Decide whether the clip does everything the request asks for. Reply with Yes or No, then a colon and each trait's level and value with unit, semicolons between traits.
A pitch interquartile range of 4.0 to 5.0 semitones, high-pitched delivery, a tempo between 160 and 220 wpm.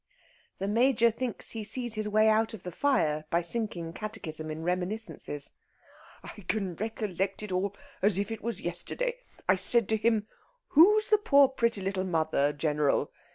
Yes: average, 4.5 semitones; high, 210 Hz; average, 165 wpm